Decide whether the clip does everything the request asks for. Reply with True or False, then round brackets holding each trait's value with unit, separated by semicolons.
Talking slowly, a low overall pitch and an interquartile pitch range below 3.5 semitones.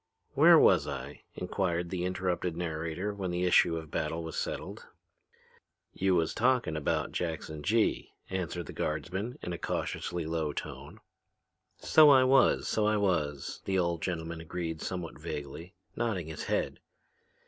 False (150 wpm; 90 Hz; 2.8 semitones)